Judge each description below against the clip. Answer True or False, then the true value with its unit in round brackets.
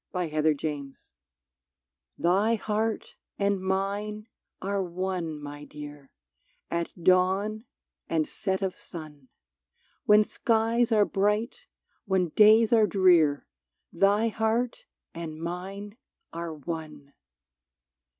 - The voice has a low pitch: False (190 Hz)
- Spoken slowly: True (100 wpm)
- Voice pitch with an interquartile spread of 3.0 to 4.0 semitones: False (4.8 semitones)